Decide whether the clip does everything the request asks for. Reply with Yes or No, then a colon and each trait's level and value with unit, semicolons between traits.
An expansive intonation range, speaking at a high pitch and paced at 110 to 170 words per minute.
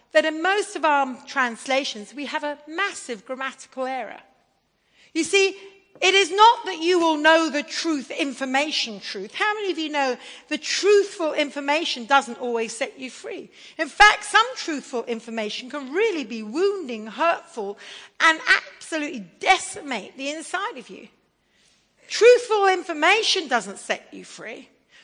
Yes: wide, 6.4 semitones; very high, 310 Hz; average, 145 wpm